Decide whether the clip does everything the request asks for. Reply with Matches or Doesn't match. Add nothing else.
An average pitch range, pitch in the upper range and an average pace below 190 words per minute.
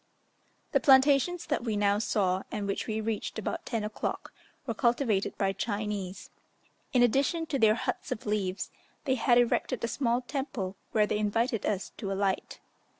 Matches